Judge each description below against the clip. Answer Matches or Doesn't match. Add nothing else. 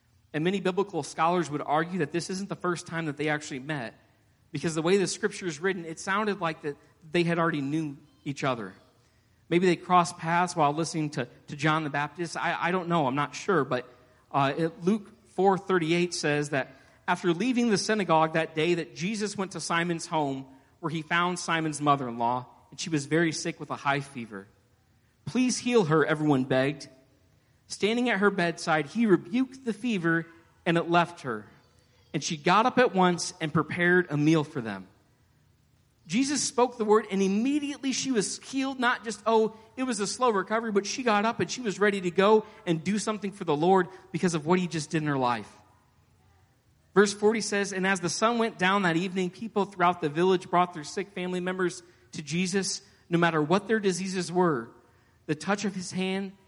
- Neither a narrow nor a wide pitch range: Matches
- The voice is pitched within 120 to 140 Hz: Doesn't match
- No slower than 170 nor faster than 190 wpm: Doesn't match